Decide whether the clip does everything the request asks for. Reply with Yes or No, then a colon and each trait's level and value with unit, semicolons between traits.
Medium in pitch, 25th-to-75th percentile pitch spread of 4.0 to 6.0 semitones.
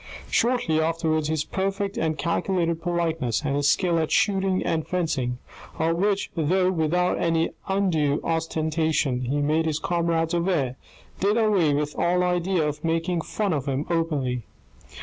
No: medium, 165 Hz; average, 2.9 semitones